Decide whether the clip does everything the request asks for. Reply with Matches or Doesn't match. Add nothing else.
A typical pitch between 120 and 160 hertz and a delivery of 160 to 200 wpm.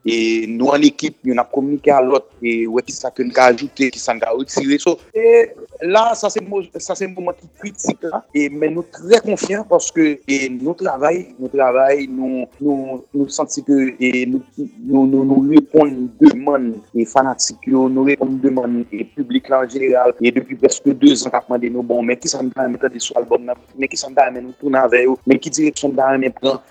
Matches